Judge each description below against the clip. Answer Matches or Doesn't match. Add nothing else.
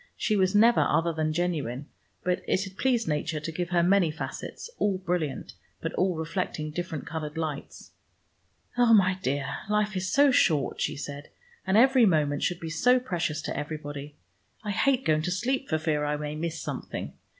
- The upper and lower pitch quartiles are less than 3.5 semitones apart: Doesn't match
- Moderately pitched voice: Matches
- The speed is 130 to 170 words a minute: Doesn't match